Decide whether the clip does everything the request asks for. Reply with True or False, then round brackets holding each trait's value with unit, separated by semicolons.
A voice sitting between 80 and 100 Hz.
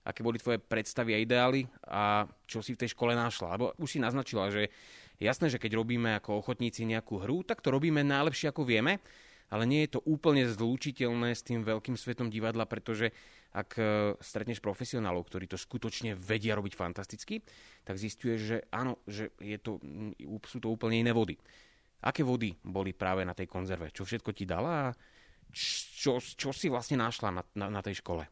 False (115 Hz)